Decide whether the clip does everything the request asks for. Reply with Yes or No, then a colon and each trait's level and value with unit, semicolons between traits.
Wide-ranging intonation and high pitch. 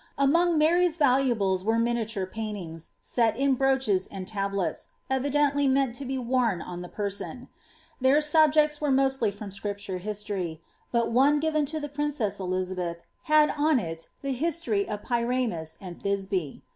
Yes: wide, 6.2 semitones; high, 235 Hz